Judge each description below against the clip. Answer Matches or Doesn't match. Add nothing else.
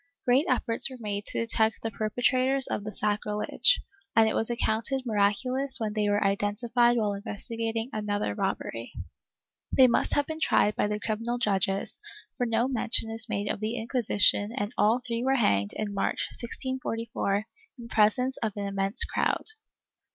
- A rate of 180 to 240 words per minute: Doesn't match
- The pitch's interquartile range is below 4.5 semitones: Matches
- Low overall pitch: Doesn't match